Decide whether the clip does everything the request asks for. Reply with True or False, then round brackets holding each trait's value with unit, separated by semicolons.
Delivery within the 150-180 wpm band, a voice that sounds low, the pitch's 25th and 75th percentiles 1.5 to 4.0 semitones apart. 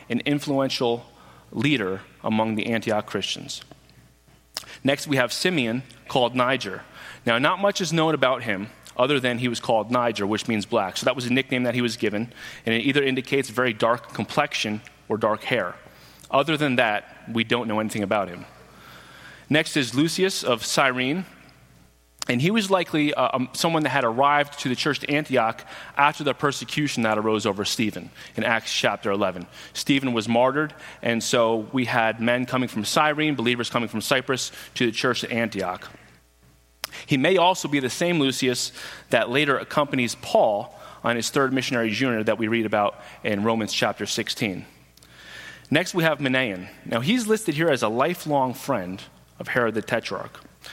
False (175 wpm; 125 Hz; 4.4 semitones)